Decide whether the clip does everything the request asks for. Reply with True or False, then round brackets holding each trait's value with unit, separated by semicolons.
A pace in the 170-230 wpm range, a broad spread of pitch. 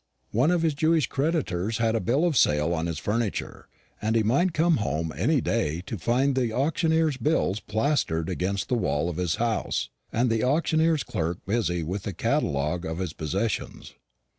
True (180 wpm; 8.3 semitones)